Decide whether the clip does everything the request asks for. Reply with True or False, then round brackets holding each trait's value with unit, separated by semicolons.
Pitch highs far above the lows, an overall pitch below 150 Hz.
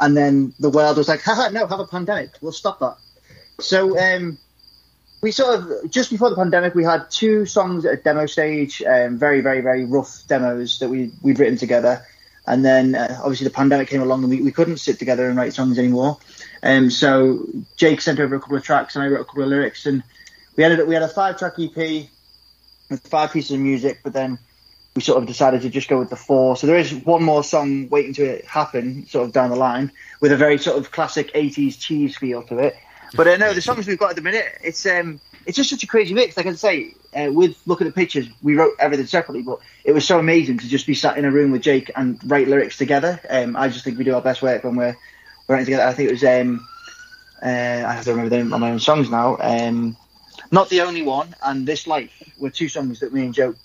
False (4.3 semitones; 140 Hz)